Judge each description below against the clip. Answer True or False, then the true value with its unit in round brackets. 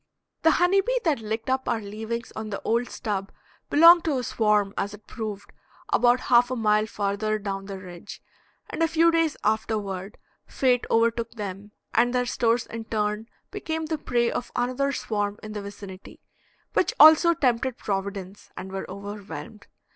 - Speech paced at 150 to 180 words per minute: True (170 wpm)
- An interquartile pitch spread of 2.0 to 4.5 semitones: True (3.8 semitones)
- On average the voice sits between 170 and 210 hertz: False (220 Hz)